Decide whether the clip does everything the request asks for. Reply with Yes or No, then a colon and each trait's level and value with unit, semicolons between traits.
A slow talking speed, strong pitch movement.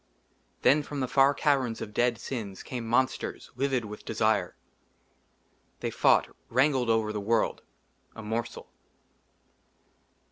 No: slow, 120 wpm; average, 3.3 semitones